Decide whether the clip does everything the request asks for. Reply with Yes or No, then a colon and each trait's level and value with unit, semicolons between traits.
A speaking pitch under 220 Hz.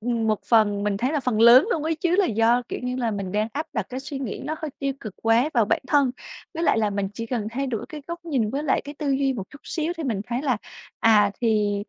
No: high, 245 Hz